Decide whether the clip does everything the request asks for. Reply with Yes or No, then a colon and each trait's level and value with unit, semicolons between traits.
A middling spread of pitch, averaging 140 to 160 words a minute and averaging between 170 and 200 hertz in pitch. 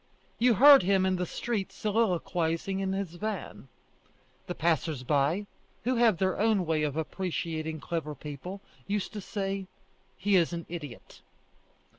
Yes: average, 3.9 semitones; average, 145 wpm; medium, 185 Hz